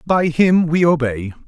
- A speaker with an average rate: Yes, average, 165 wpm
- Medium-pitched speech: Yes, medium, 155 Hz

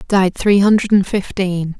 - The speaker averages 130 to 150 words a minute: Yes, slow, 135 wpm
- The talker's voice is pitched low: No, high, 195 Hz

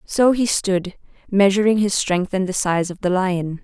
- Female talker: Yes, female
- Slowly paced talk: No, average, 200 wpm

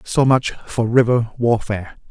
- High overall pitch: No, low, 120 Hz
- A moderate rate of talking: Yes, average, 145 wpm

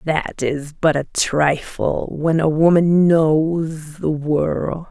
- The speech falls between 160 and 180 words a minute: No, slow, 135 wpm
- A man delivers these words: No, female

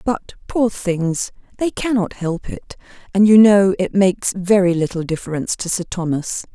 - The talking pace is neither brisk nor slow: Yes, average, 165 wpm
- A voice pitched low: No, high, 190 Hz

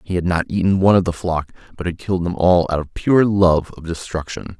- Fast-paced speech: Yes, fast, 250 wpm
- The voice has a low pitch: Yes, very low, 90 Hz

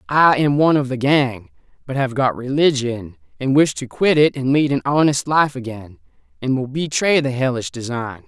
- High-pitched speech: No, low, 135 Hz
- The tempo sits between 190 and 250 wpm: Yes, average, 195 wpm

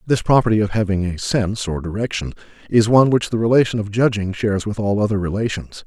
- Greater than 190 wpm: Yes, fast, 205 wpm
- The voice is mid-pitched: No, low, 105 Hz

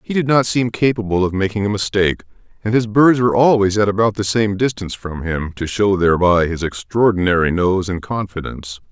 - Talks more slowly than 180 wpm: No, average, 195 wpm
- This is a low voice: Yes, low, 100 Hz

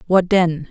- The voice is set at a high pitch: No, medium, 175 Hz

